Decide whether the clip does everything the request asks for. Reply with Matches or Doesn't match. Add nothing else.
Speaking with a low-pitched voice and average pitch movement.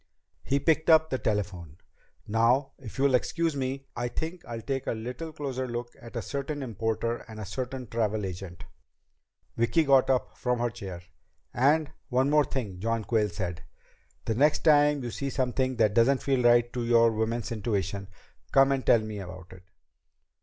Matches